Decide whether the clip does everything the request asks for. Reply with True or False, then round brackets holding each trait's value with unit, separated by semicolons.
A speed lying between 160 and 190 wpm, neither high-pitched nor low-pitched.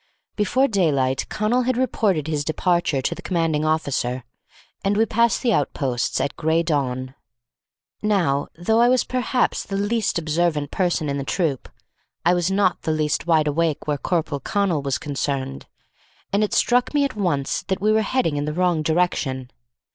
True (170 wpm; 165 Hz)